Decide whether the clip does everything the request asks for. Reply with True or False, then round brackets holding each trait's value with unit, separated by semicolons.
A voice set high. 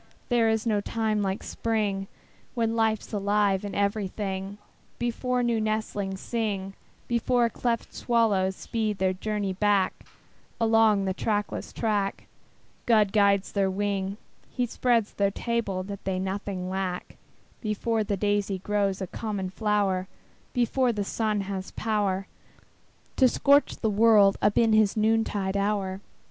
True (205 Hz)